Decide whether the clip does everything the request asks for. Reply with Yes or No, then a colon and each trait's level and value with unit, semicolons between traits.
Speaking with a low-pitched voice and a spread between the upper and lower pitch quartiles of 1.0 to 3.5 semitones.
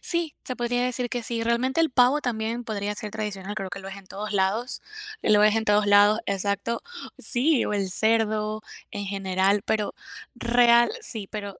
No: high, 215 Hz; average, 3.0 semitones